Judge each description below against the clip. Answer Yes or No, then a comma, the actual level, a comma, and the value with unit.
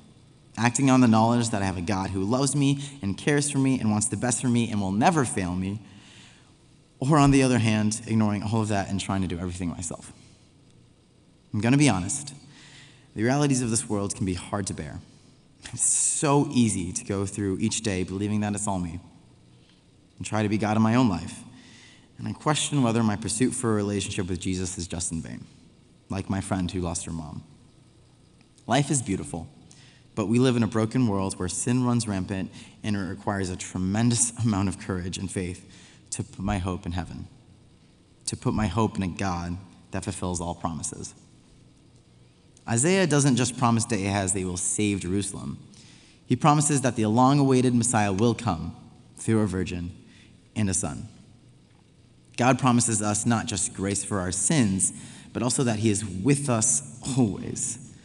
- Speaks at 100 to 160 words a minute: No, average, 190 wpm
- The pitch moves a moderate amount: Yes, average, 4.5 semitones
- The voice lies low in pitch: Yes, low, 105 Hz